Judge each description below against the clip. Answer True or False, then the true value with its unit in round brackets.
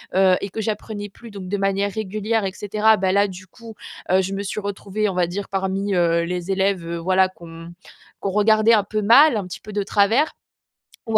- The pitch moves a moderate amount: False (2.2 semitones)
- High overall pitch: True (200 Hz)